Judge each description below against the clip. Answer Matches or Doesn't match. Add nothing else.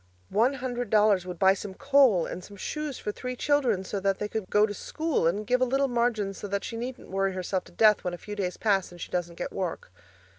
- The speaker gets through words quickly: Matches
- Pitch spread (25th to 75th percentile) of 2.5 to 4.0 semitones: Doesn't match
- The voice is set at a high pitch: Matches